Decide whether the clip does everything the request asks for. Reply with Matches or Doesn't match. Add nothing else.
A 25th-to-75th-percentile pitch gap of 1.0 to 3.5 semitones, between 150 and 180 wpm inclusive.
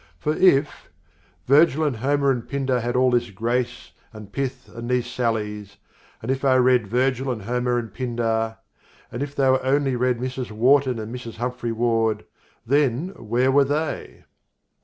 Matches